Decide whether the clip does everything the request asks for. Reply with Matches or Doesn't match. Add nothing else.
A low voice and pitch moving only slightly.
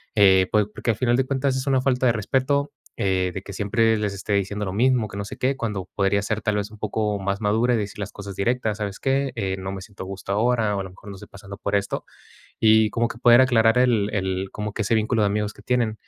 Doesn't match